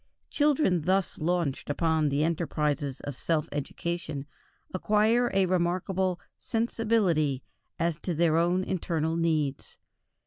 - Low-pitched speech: No, medium, 170 Hz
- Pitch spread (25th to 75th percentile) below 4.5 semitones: Yes, average, 3.5 semitones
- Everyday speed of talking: No, slow, 110 wpm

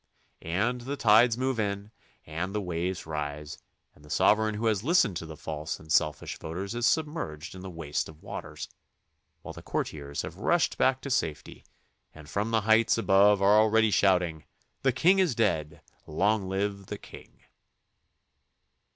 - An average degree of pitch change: No, wide, 6.0 semitones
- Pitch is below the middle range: Yes, low, 100 Hz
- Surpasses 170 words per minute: No, average, 165 wpm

